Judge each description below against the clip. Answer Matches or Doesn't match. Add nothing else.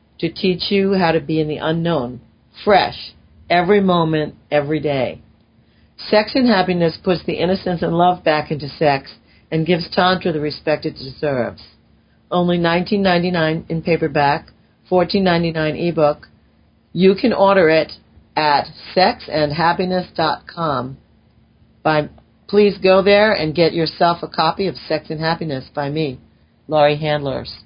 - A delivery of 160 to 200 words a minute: Doesn't match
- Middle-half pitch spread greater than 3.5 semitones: Doesn't match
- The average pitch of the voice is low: Doesn't match